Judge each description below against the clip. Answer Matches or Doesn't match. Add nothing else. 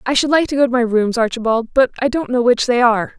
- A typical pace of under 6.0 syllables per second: Doesn't match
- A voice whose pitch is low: Doesn't match